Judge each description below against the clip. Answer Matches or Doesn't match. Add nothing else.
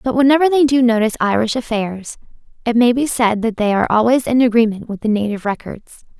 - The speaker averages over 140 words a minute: Matches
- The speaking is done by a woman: Matches